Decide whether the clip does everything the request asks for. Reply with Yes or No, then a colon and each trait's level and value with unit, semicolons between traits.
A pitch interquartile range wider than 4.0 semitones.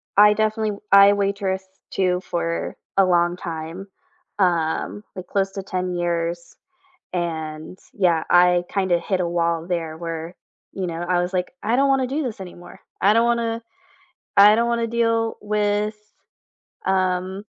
No: average, 3.3 semitones